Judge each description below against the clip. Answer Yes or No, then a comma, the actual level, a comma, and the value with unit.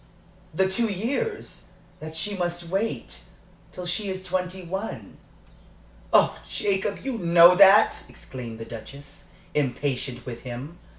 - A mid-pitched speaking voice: Yes, medium, 180 Hz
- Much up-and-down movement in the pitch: Yes, wide, 5.7 semitones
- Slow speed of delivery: Yes, slow, 125 wpm